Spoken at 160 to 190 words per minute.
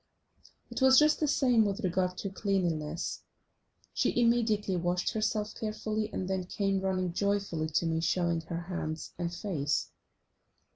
No: average, 145 wpm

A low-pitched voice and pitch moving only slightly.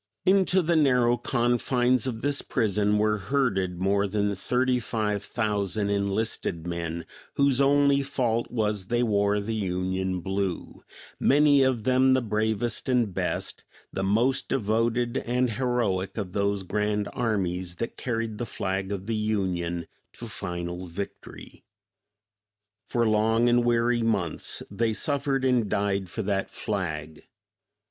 No: low, 110 Hz; average, 3.9 semitones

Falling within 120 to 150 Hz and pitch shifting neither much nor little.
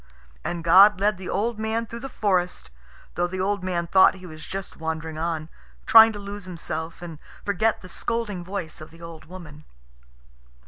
No: medium, 185 Hz; average, 3.7 semitones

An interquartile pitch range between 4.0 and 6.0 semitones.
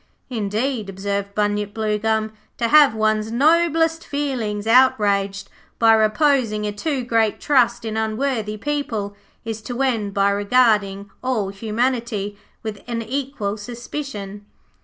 No: average, 3.6 semitones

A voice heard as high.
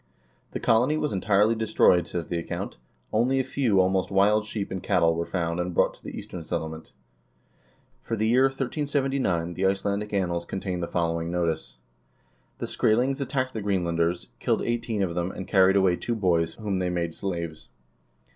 No: very low, 95 Hz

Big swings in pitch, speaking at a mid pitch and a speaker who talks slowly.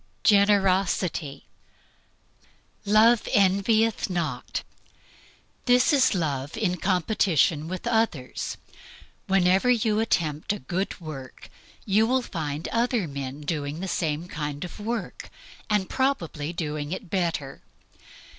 Yes: wide, 5.8 semitones; medium, 180 Hz; slow, 110 wpm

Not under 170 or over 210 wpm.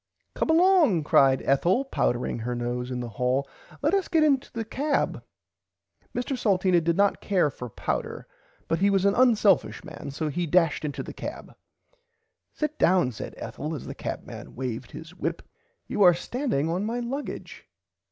Yes: average, 175 wpm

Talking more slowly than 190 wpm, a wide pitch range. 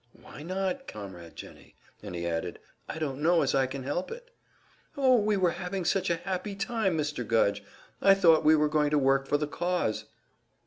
No: average, 195 wpm; wide, 6.0 semitones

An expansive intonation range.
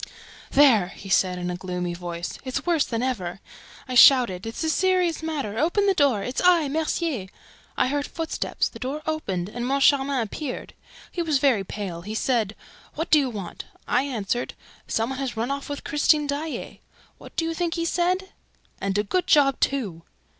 Yes: wide, 7.1 semitones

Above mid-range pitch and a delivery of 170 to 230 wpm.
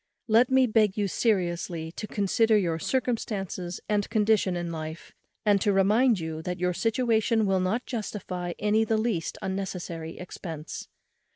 No: high, 195 Hz; average, 145 wpm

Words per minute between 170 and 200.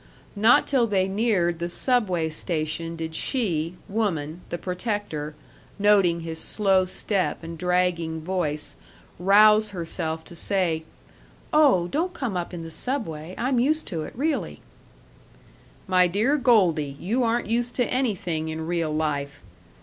No: average, 140 wpm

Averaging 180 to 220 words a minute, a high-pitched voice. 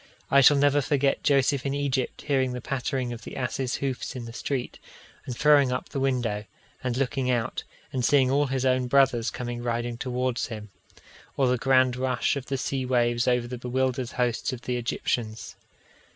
No: average, 185 wpm; low, 130 Hz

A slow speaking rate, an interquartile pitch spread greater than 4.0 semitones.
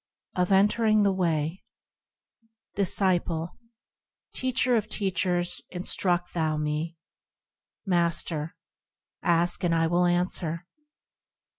No: slow, 95 wpm; narrow, 2.5 semitones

